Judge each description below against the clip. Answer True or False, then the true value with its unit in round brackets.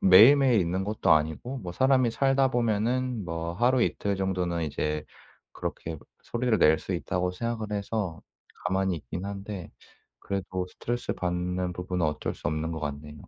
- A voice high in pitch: False (95 Hz)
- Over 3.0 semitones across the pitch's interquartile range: True (5.3 semitones)